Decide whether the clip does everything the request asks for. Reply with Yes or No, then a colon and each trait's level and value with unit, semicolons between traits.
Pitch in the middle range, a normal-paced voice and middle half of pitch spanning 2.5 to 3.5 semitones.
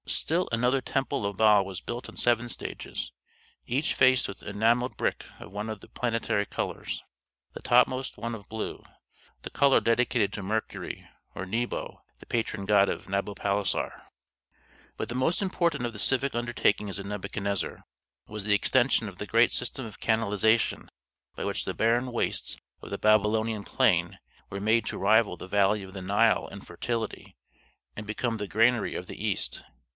No: low, 110 Hz; average, 170 wpm; average, 3.0 semitones